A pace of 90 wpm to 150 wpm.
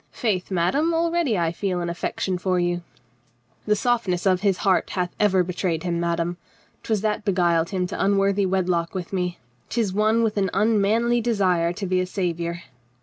No: average, 180 wpm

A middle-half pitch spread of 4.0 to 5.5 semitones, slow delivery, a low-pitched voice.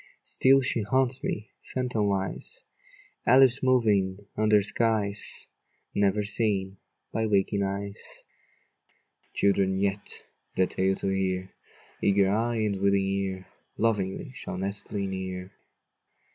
No: narrow, 2.5 semitones; slow, 105 wpm; low, 100 Hz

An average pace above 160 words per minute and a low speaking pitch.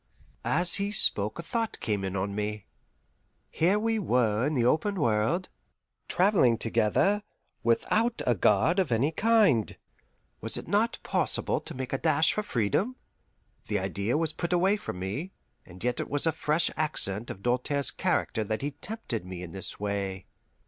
Yes: average, 170 wpm; low, 130 Hz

